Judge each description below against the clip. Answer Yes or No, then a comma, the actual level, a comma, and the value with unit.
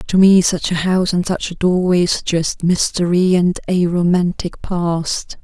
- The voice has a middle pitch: Yes, medium, 175 Hz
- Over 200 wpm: No, average, 165 wpm